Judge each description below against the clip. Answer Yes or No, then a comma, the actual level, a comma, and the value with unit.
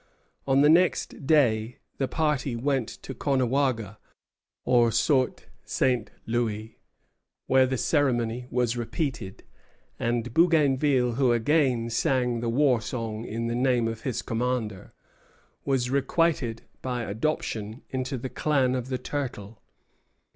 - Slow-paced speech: Yes, slow, 125 wpm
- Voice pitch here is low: Yes, low, 125 Hz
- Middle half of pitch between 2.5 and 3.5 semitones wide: Yes, average, 2.8 semitones